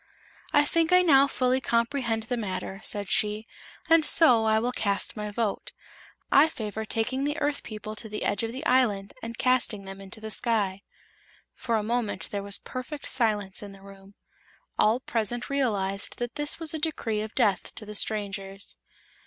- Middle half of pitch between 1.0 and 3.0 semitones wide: No, average, 3.8 semitones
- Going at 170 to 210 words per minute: Yes, average, 180 wpm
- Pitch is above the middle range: Yes, high, 225 Hz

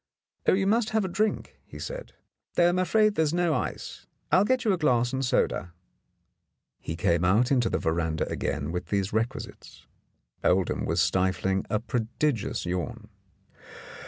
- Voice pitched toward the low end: Yes, low, 120 Hz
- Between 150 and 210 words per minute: Yes, average, 160 wpm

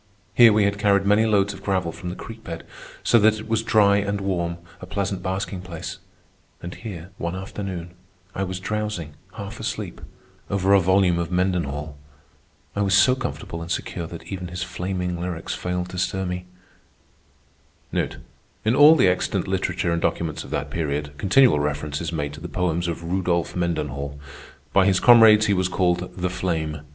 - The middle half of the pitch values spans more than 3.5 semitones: No, average, 2.9 semitones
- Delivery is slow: No, average, 180 wpm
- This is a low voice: Yes, very low, 90 Hz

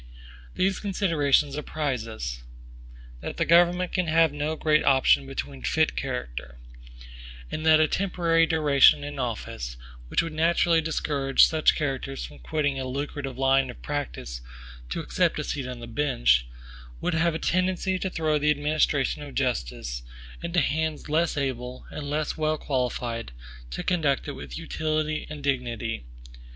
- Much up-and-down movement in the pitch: No, average, 3.7 semitones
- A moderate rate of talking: Yes, average, 150 wpm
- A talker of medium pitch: Yes, medium, 145 Hz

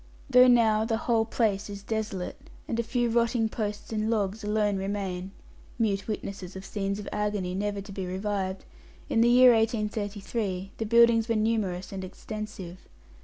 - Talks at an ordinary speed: Yes, average, 165 wpm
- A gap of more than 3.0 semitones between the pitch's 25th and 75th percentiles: No, narrow, 2.4 semitones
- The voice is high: Yes, high, 210 Hz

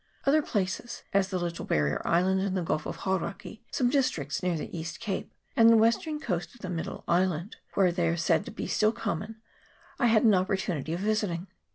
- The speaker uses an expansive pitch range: No, average, 4.2 semitones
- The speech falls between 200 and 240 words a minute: Yes, fast, 205 wpm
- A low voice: No, high, 190 Hz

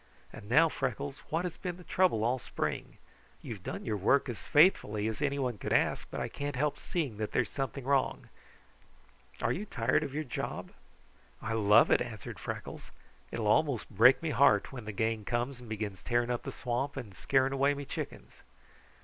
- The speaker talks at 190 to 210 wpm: Yes, average, 200 wpm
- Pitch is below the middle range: Yes, low, 125 Hz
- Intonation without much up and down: No, average, 4.2 semitones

